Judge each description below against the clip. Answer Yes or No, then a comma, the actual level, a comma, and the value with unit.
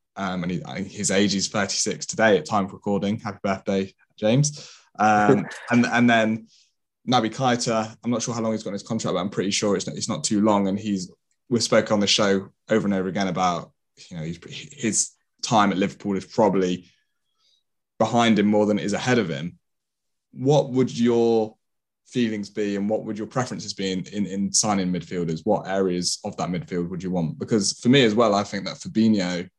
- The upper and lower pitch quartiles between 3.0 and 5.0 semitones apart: No, narrow, 2.6 semitones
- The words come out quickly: Yes, fast, 210 wpm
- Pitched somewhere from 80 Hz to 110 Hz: Yes, low, 105 Hz